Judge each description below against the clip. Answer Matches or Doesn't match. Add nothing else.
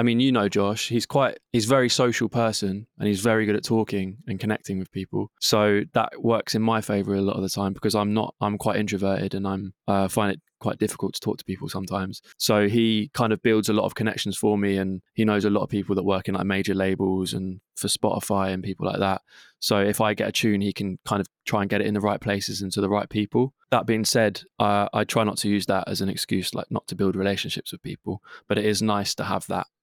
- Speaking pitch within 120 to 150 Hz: Doesn't match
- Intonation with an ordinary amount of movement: Doesn't match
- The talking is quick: Matches